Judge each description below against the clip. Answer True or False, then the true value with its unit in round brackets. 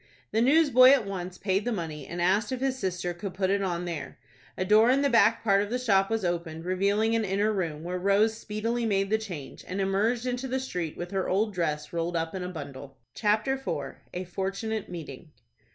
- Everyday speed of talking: False (215 wpm)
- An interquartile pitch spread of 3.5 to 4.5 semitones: True (4.1 semitones)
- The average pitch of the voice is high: True (195 Hz)